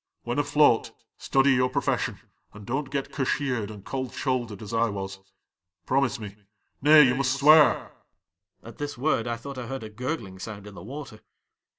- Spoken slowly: No, average, 195 wpm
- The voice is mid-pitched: No, low, 125 Hz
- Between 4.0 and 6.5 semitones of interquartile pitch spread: Yes, average, 4.5 semitones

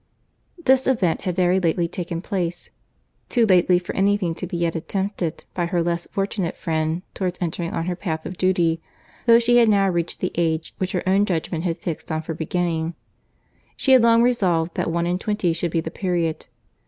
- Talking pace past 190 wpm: Yes, average, 200 wpm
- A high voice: No, medium, 175 Hz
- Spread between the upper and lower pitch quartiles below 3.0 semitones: Yes, narrow, 2.6 semitones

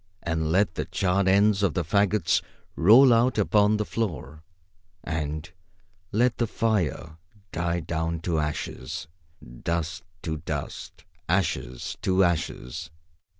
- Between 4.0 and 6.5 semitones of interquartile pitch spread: Yes, average, 4.5 semitones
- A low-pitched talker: Yes, very low, 85 Hz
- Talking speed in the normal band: No, slow, 120 wpm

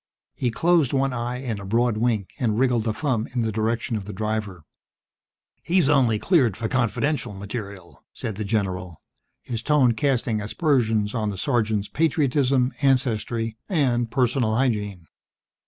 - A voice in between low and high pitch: No, low, 115 Hz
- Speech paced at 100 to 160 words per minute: Yes, average, 150 wpm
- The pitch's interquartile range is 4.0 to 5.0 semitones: No, average, 3.6 semitones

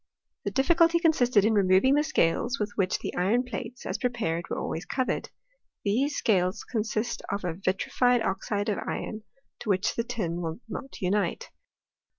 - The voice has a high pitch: Yes, high, 215 Hz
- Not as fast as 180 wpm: Yes, average, 165 wpm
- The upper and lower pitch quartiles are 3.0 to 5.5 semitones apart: Yes, average, 4.7 semitones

